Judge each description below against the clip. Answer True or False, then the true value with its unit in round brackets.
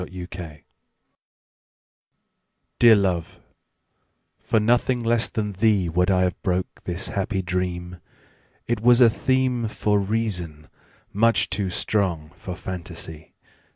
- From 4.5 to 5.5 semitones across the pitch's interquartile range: False (4.0 semitones)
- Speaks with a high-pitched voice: False (95 Hz)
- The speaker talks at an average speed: False (105 wpm)